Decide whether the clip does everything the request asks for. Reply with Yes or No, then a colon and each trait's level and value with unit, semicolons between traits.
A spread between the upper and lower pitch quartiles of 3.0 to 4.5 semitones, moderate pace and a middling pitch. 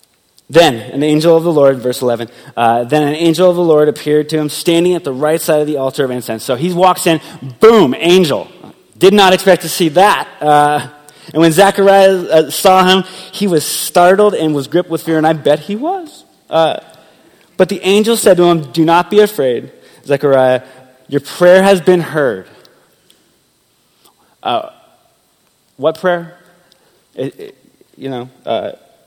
Yes: average, 4.1 semitones; average, 175 wpm; medium, 165 Hz